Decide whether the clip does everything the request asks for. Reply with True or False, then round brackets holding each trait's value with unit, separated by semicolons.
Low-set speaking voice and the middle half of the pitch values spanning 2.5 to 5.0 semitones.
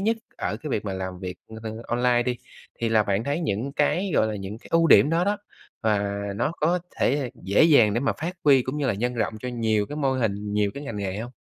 False (120 Hz; 5.6 semitones)